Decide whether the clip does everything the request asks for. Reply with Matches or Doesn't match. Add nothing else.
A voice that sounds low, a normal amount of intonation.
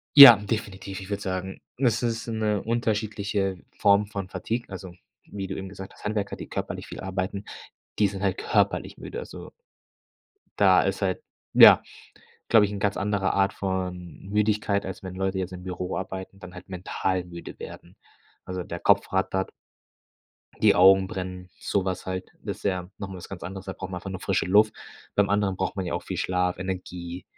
Doesn't match